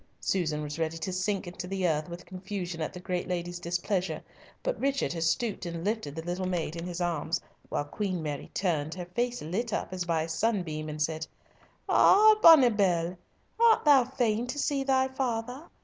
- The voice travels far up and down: Yes, wide, 5.7 semitones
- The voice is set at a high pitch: No, medium, 180 Hz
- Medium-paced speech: Yes, average, 190 wpm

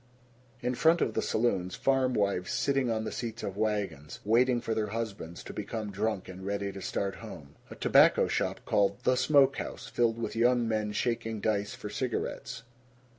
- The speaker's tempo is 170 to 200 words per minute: Yes, average, 175 wpm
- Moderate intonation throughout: Yes, average, 3.2 semitones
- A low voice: Yes, low, 110 Hz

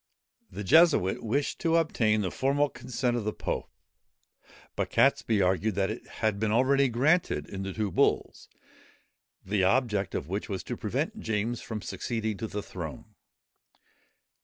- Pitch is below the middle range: Yes, low, 110 Hz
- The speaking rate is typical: Yes, average, 160 wpm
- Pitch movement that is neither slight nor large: Yes, average, 4.4 semitones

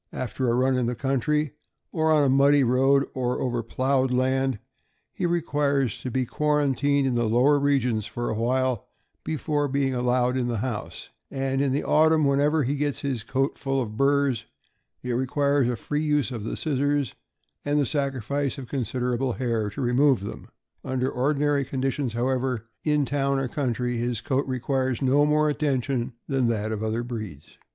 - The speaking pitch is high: No, low, 130 Hz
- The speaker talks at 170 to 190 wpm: Yes, average, 175 wpm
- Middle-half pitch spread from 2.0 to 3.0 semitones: Yes, narrow, 2.5 semitones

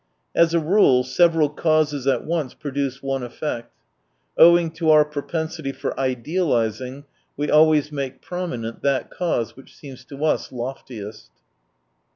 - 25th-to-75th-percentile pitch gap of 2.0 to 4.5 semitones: Yes, average, 3.6 semitones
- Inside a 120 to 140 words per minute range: Yes, slow, 135 wpm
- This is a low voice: No, medium, 145 Hz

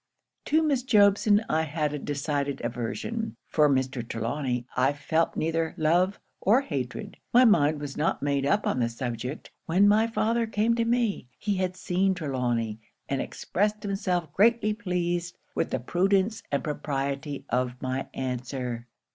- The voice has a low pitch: No, medium, 160 Hz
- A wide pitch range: Yes, wide, 7.3 semitones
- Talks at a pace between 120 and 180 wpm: Yes, average, 155 wpm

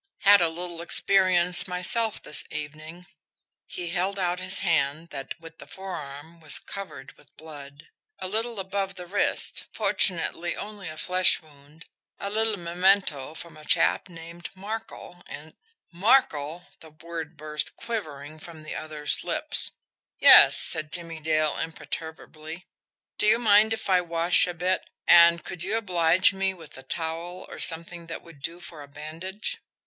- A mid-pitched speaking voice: Yes, medium, 170 Hz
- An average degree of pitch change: Yes, average, 3.1 semitones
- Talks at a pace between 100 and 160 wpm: Yes, average, 155 wpm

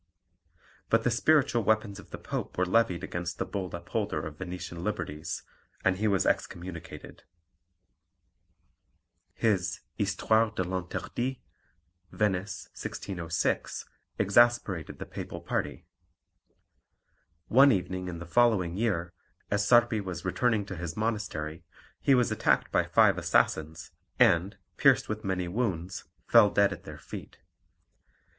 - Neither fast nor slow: No, slow, 125 wpm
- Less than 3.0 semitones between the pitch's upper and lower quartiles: No, average, 4.1 semitones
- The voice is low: Yes, very low, 95 Hz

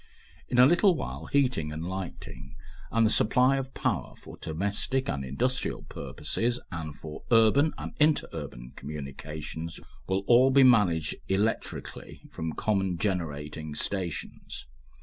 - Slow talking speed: Yes, slow, 130 wpm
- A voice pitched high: No, very low, 95 Hz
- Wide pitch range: Yes, wide, 8.3 semitones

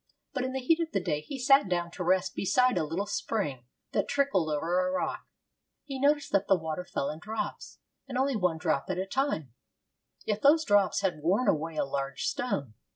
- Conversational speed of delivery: No, fast, 210 wpm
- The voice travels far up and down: Yes, wide, 8.3 semitones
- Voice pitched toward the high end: Yes, high, 195 Hz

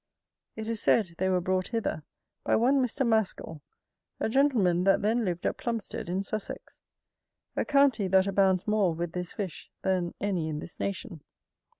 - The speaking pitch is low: No, high, 195 Hz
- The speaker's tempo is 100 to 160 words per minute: No, average, 170 wpm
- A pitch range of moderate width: Yes, average, 3.8 semitones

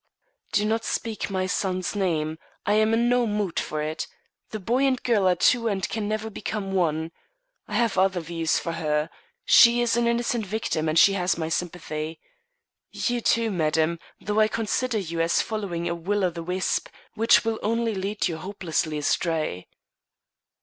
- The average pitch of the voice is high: Yes, high, 195 Hz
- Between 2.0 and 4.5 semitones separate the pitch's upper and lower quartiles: No, average, 5.0 semitones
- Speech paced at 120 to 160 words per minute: No, average, 175 wpm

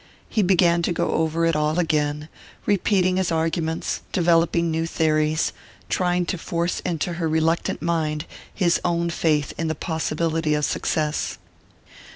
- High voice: No, medium, 165 Hz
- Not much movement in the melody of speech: Yes, narrow, 1.6 semitones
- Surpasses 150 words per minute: No, average, 145 wpm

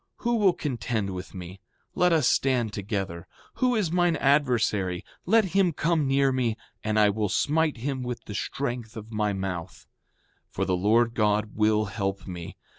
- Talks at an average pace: Yes, average, 175 wpm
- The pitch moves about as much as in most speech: No, wide, 6.0 semitones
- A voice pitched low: Yes, low, 115 Hz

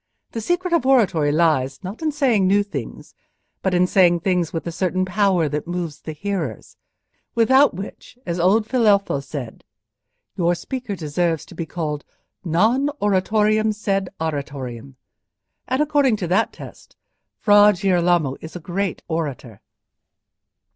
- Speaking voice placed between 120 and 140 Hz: No, medium, 180 Hz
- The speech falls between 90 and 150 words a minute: Yes, average, 140 wpm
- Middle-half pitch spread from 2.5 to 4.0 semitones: No, average, 4.8 semitones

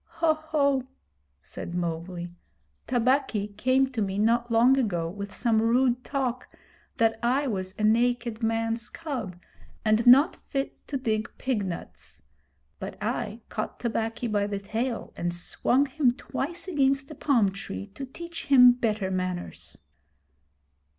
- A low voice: No, high, 235 Hz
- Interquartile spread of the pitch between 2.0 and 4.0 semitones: No, average, 4.5 semitones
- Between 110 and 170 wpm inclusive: Yes, average, 140 wpm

